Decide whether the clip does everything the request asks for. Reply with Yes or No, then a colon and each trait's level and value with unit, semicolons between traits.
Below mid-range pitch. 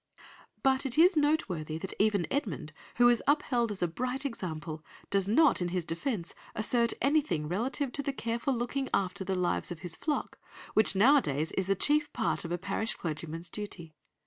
No: high, 210 Hz